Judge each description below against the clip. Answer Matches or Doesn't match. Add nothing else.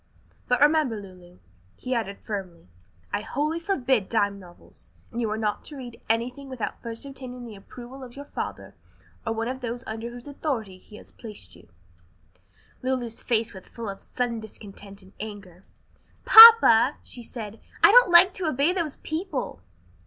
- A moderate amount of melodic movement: Matches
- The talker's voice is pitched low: Doesn't match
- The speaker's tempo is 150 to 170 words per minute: Matches